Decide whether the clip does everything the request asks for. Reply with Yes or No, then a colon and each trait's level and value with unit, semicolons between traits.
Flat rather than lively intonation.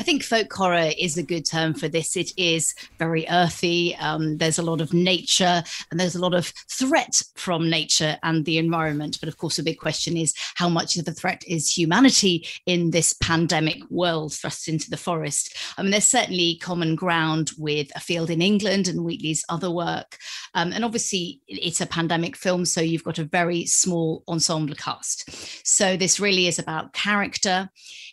Yes: narrow, 2.0 semitones